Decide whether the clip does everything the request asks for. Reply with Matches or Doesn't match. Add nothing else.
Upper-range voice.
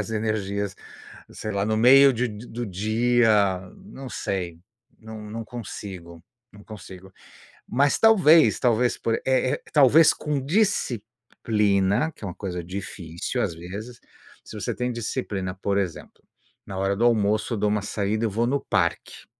Doesn't match